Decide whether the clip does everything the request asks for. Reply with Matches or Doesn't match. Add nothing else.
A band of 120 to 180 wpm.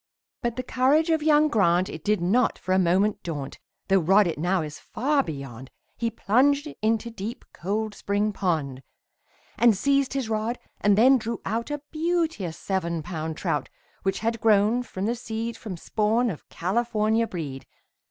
Matches